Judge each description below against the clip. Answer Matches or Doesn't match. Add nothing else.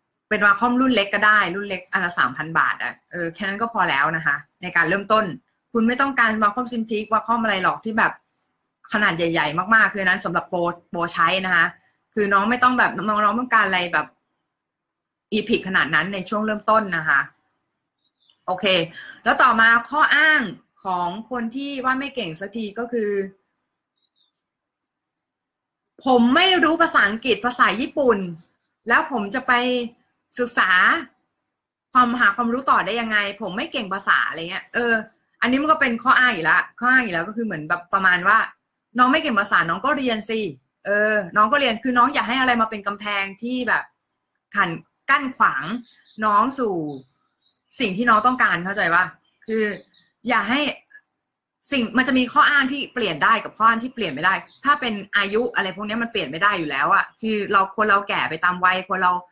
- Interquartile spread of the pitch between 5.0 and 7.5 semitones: Doesn't match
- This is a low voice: Doesn't match